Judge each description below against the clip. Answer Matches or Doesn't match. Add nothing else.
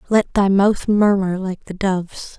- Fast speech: Doesn't match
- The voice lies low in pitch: Doesn't match